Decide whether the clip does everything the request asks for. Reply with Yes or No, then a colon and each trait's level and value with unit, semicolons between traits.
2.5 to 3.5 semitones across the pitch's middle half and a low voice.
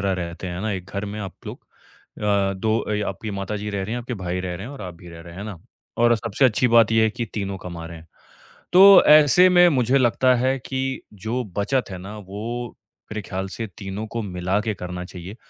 No: average, 4.0 semitones; low, 105 Hz